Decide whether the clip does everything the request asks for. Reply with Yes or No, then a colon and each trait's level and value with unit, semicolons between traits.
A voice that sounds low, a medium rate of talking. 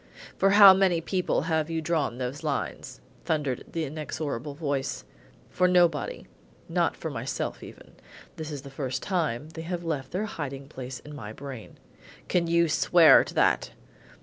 No: medium, 155 Hz; average, 160 wpm